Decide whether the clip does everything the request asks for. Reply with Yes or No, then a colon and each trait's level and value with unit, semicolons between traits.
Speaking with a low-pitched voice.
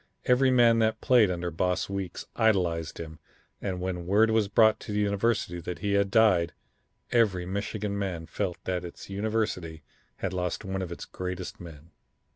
Yes: very low, 95 Hz